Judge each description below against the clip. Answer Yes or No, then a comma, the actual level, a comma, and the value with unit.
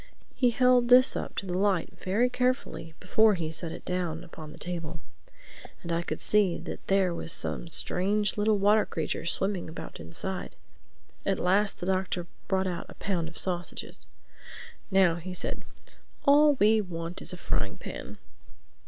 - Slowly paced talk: No, average, 165 wpm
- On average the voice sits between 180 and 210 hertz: Yes, medium, 185 Hz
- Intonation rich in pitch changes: No, average, 3.6 semitones